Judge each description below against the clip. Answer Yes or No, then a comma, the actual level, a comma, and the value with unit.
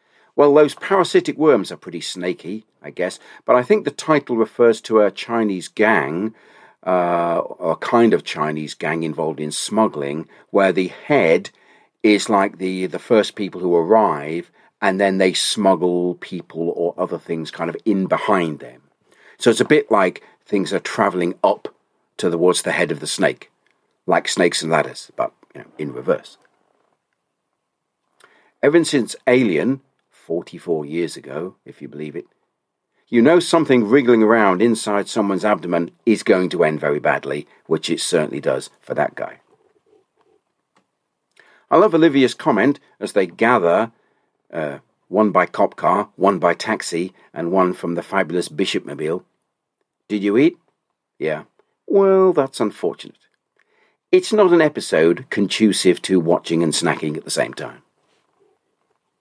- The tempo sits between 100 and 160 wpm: Yes, average, 150 wpm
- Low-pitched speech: Yes, low, 105 Hz